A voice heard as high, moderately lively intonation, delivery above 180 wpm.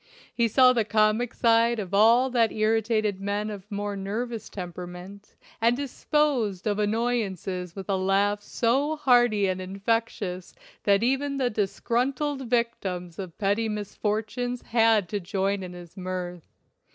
No: high, 210 Hz; average, 3.4 semitones; average, 140 wpm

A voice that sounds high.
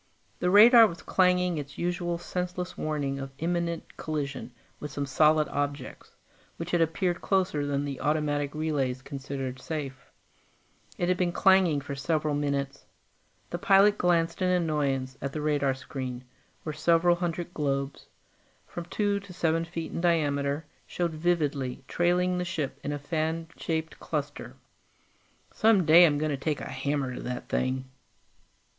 No: medium, 155 Hz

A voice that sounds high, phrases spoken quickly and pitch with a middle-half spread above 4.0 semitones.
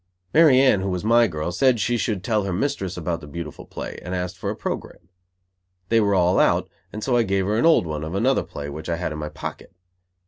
No: very low, 95 Hz; fast, 245 wpm; average, 5.3 semitones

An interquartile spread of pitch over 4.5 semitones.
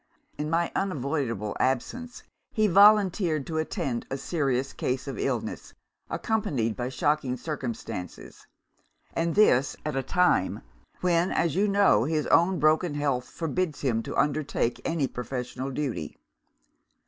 Yes: average, 5.1 semitones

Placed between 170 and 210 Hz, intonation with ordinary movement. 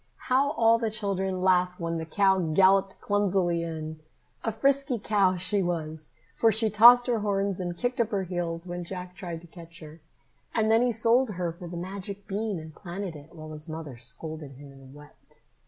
Yes: medium, 185 Hz; average, 4.1 semitones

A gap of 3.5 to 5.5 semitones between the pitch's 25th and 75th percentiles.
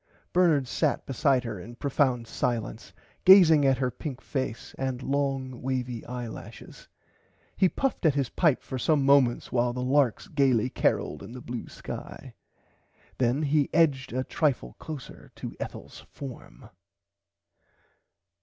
No: average, 2.7 semitones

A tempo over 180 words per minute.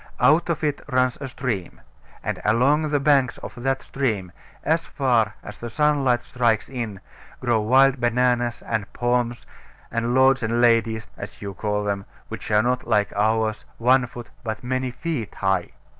No: average, 165 wpm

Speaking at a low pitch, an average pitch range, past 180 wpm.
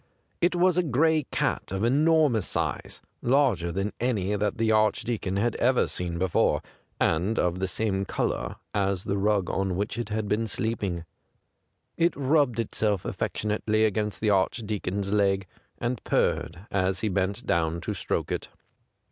No: low, 105 Hz; average, 3.6 semitones; average, 160 wpm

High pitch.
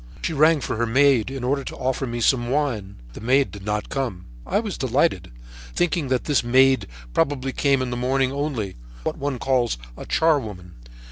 No: low, 130 Hz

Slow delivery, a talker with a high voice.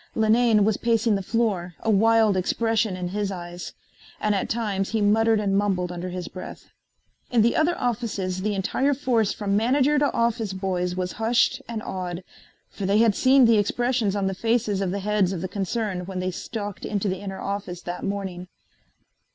No: average, 190 wpm; high, 205 Hz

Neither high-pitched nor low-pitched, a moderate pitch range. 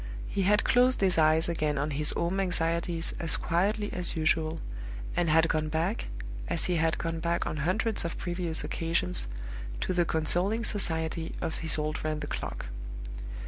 No: medium, 165 Hz; narrow, 2.3 semitones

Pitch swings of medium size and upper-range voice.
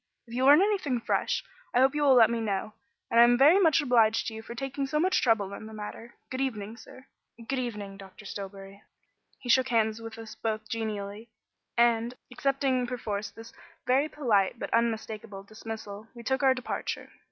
Yes: average, 3.3 semitones; high, 230 Hz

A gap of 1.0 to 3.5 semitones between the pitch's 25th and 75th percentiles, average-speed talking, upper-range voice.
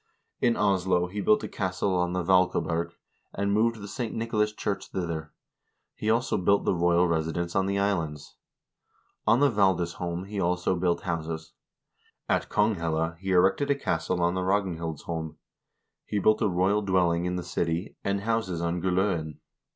No: average, 3.1 semitones; average, 160 wpm; very low, 90 Hz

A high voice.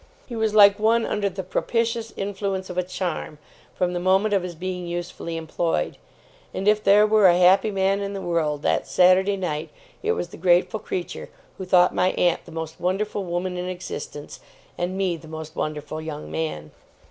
No: medium, 180 Hz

